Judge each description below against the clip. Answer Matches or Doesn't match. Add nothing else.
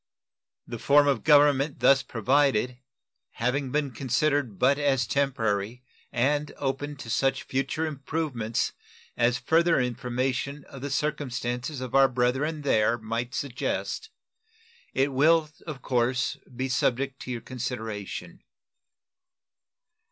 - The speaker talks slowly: Matches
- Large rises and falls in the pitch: Doesn't match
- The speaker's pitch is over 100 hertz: Matches